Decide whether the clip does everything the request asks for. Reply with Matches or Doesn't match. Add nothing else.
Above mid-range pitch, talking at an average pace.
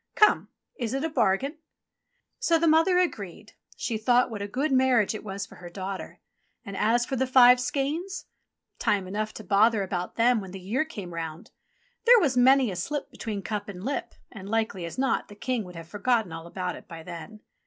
Doesn't match